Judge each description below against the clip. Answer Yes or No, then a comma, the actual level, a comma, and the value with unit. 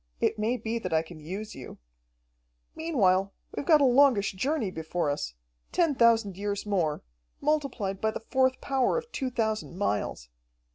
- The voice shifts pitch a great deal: Yes, wide, 5.8 semitones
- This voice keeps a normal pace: Yes, average, 160 wpm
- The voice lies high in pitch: Yes, high, 220 Hz